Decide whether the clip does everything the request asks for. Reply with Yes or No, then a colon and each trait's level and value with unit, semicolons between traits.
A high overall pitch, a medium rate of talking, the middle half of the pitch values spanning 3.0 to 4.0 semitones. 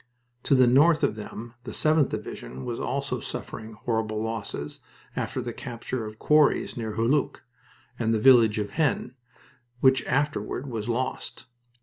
No: low, 115 Hz; average, 150 wpm; average, 3.5 semitones